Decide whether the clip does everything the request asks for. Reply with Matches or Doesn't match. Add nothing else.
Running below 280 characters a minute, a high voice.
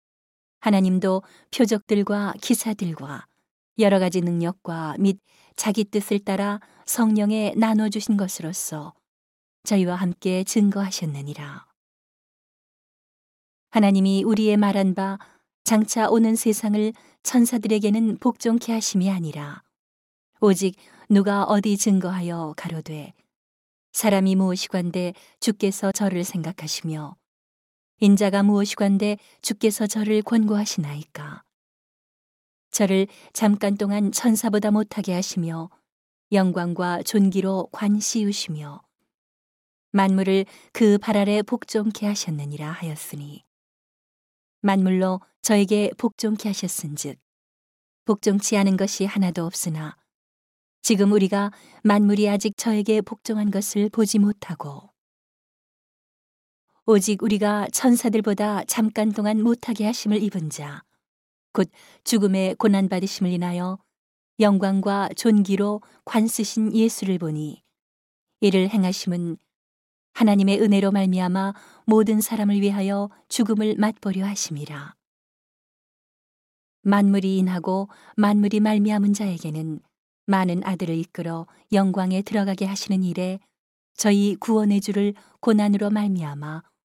Matches